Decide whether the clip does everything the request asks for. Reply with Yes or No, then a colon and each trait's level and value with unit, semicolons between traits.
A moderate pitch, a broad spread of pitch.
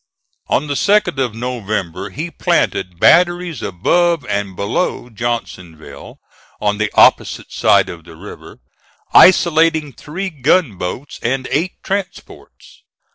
No: low, 125 Hz; wide, 8.9 semitones